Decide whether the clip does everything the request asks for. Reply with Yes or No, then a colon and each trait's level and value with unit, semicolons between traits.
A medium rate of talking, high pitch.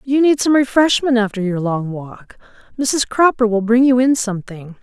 Yes: average, 185 wpm; high, 235 Hz